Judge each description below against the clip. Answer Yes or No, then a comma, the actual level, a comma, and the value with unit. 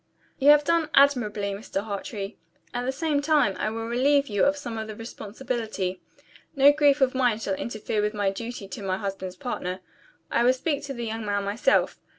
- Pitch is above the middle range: Yes, high, 225 Hz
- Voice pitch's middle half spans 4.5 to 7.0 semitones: Yes, average, 5.2 semitones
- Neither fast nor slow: Yes, average, 195 wpm